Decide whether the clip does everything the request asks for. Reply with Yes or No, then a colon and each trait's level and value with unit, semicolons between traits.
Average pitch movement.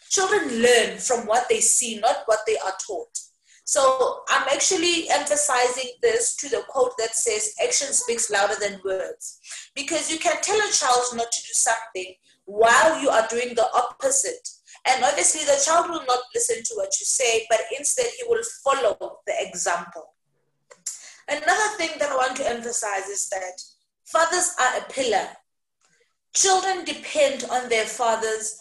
No: wide, 7.1 semitones